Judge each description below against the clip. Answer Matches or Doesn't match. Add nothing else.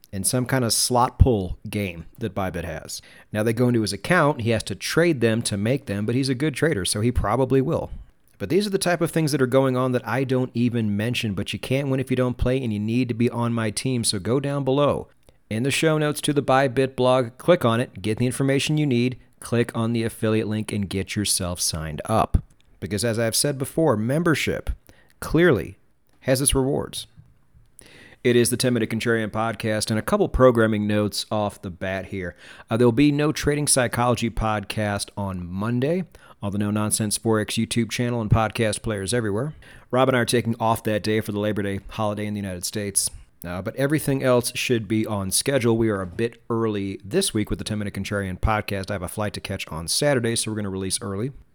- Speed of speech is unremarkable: Doesn't match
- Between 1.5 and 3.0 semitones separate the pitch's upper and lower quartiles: Doesn't match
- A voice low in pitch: Matches